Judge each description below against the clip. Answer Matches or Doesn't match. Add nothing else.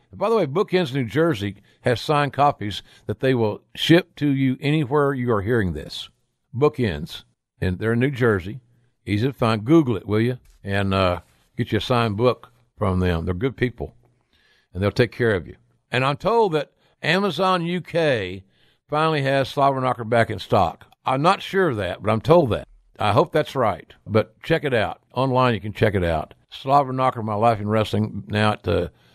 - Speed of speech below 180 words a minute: Doesn't match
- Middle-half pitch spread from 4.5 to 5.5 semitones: Matches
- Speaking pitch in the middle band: Doesn't match